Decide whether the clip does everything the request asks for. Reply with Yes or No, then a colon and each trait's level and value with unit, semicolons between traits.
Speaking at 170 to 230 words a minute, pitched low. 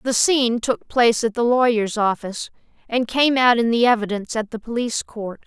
No: average, 200 wpm; high, 230 Hz